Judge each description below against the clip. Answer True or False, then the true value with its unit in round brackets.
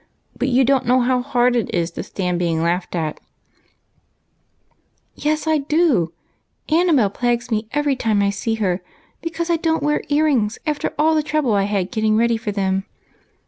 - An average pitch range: False (6.9 semitones)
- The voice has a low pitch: False (240 Hz)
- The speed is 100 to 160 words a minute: False (185 wpm)